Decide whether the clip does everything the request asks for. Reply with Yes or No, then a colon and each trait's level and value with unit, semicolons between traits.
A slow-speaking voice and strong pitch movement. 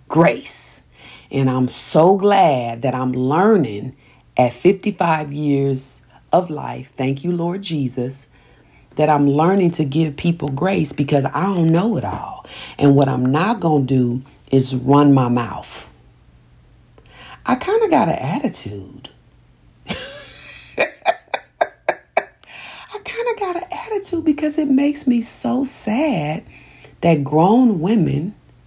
Yes: slow, 130 wpm; wide, 8.1 semitones